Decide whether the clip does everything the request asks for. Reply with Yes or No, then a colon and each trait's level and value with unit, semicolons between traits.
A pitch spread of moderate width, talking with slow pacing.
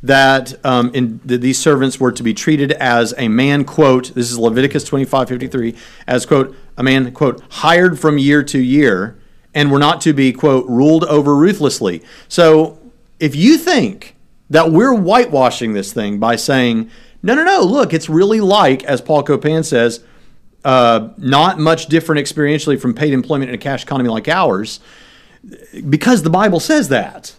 No: average, 3.8 semitones; average, 175 wpm